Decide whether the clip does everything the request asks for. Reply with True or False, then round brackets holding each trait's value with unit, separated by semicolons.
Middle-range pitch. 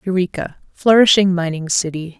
True (180 Hz)